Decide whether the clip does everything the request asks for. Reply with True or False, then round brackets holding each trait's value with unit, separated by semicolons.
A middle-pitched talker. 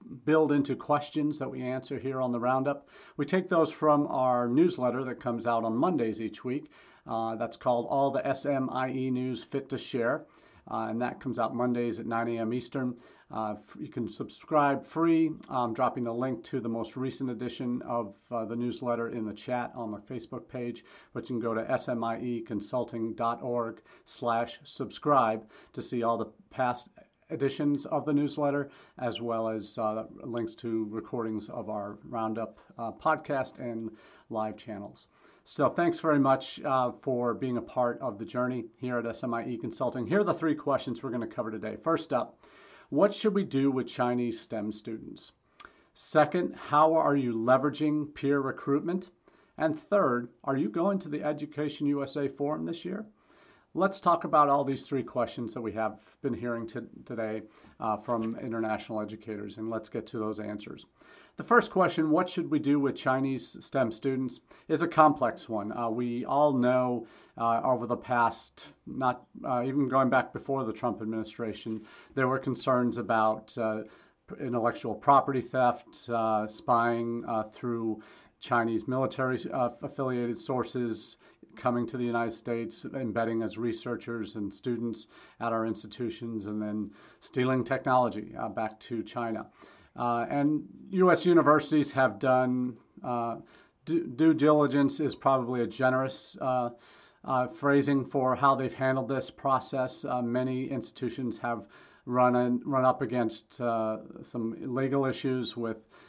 False (125 Hz)